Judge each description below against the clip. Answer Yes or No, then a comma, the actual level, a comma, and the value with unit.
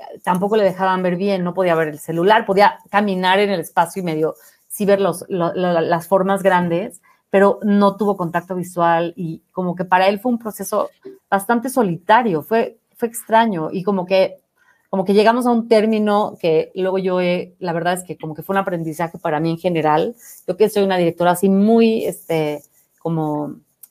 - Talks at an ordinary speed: No, fast, 195 wpm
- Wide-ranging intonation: No, average, 3.4 semitones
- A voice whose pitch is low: No, high, 190 Hz